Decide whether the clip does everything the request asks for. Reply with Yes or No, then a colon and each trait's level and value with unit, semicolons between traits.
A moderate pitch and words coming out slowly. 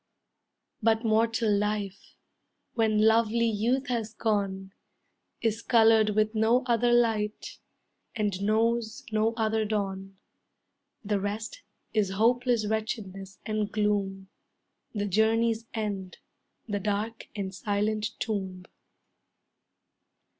No: high, 215 Hz; slow, 100 wpm